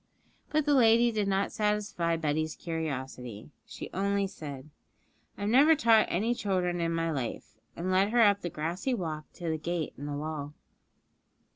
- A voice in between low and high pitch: Yes, medium, 175 Hz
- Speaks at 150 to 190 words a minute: Yes, average, 170 wpm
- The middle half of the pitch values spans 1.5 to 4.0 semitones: No, average, 5.2 semitones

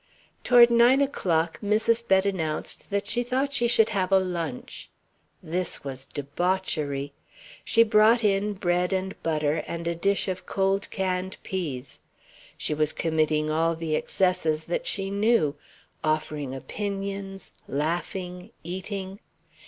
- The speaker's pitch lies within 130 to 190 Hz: Yes, medium, 185 Hz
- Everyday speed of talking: No, slow, 130 wpm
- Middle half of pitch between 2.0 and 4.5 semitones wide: Yes, average, 4.1 semitones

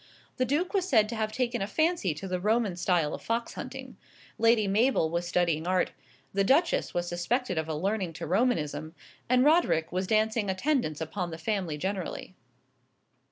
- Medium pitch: No, high, 195 Hz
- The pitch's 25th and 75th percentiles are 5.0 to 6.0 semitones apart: Yes, wide, 5.5 semitones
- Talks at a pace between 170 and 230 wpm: Yes, average, 175 wpm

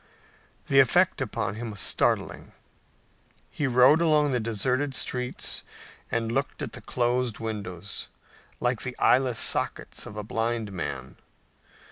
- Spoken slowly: Yes, slow, 130 wpm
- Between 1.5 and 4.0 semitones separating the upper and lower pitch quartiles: Yes, average, 3.5 semitones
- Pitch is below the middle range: Yes, low, 120 Hz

